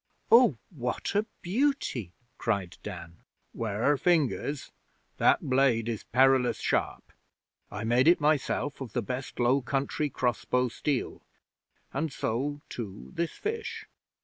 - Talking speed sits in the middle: No, slow, 125 wpm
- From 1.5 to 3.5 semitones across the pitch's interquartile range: No, average, 4.6 semitones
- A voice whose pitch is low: Yes, low, 130 Hz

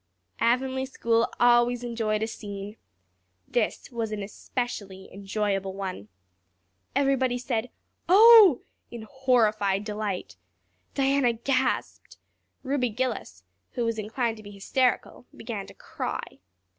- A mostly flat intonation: No, average, 3.7 semitones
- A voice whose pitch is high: Yes, high, 230 Hz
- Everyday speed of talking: No, slow, 110 wpm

